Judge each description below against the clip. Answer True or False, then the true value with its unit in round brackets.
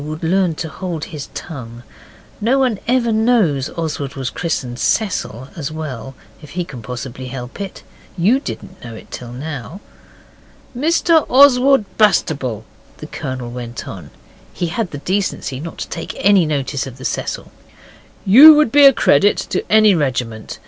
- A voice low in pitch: False (160 Hz)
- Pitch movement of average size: False (8.1 semitones)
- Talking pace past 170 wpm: False (160 wpm)